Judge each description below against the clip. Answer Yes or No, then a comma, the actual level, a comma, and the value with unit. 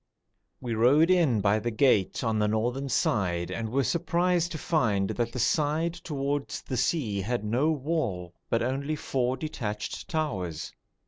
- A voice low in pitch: Yes, low, 125 Hz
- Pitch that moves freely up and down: Yes, wide, 6.1 semitones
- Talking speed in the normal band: Yes, average, 155 wpm